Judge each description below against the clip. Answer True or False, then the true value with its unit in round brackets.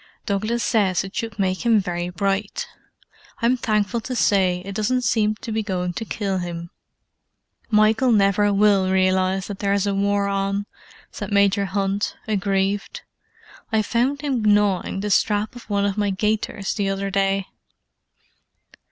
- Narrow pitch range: True (1.8 semitones)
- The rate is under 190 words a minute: True (155 wpm)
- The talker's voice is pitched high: True (200 Hz)